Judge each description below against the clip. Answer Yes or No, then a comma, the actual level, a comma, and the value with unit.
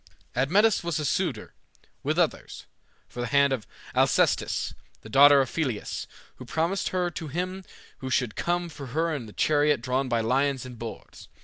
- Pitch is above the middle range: No, medium, 140 Hz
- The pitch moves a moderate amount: Yes, average, 4.8 semitones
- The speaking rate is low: No, average, 175 wpm